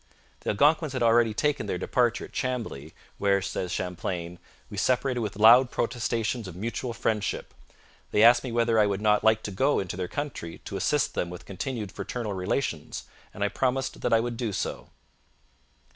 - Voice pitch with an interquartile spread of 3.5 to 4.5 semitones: Yes, average, 3.8 semitones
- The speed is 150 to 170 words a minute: No, average, 180 wpm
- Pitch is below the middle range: Yes, low, 110 Hz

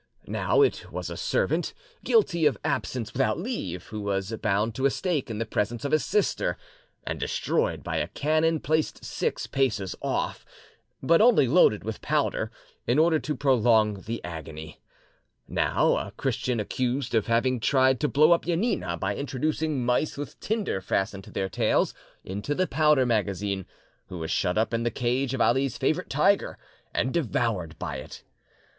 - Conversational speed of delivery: Yes, average, 170 wpm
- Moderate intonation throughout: No, wide, 6.6 semitones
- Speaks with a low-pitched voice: Yes, low, 125 Hz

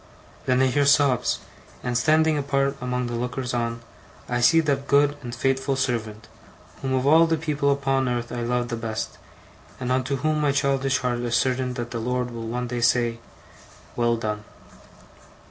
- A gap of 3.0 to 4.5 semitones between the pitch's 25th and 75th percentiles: No, narrow, 2.4 semitones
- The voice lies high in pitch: No, low, 125 Hz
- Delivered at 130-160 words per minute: No, average, 180 wpm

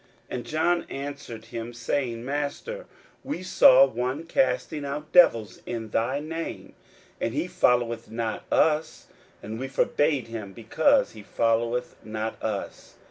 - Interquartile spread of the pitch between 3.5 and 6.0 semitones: Yes, average, 4.7 semitones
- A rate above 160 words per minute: No, slow, 135 wpm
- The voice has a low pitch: Yes, low, 125 Hz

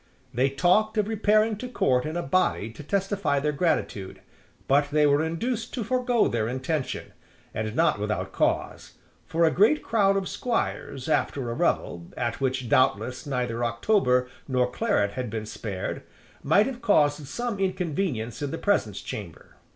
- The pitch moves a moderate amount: No, wide, 8.3 semitones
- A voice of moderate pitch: Yes, medium, 145 Hz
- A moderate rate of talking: Yes, average, 160 wpm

